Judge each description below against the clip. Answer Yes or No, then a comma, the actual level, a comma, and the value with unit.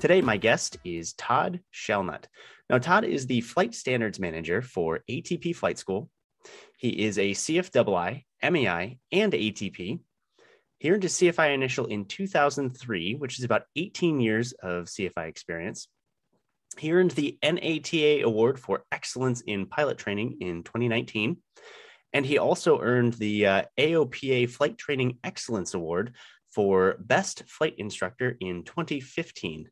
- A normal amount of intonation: No, wide, 6.6 semitones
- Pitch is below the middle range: Yes, low, 125 Hz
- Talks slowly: No, average, 145 wpm